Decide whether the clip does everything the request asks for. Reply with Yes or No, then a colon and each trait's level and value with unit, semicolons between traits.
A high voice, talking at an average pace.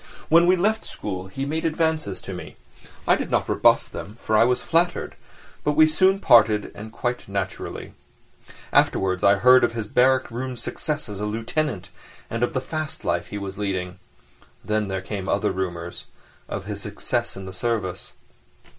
No: low, 115 Hz; average, 170 wpm